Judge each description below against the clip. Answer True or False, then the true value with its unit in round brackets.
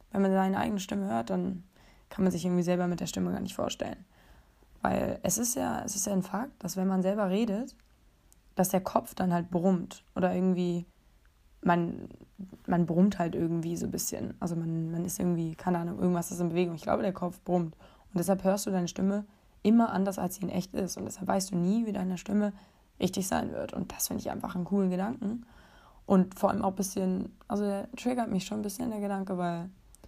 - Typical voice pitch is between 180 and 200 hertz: True (190 Hz)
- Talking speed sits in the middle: False (225 wpm)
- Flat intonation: True (2.1 semitones)